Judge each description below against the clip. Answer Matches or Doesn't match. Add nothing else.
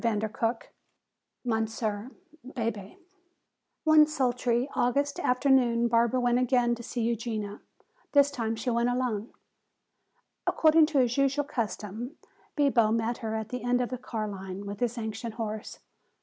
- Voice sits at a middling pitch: Doesn't match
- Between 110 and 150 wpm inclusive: Matches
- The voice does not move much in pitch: Matches